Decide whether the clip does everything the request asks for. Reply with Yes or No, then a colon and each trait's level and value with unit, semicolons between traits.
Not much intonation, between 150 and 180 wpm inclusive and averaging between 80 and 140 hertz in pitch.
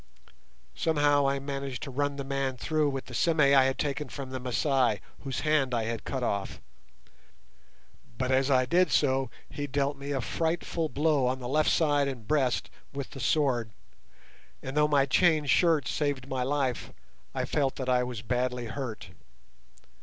Yes: narrow, 2.3 semitones; average, 175 wpm; low, 135 Hz